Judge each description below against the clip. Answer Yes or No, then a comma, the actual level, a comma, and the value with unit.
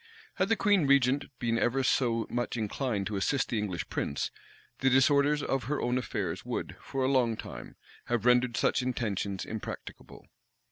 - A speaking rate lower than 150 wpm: No, average, 170 wpm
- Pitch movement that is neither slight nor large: Yes, average, 3.1 semitones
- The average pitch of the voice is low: Yes, low, 125 Hz